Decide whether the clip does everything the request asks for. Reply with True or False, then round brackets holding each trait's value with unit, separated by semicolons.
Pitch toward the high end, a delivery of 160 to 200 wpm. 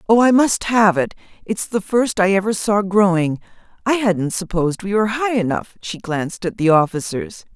True (200 Hz; 185 wpm)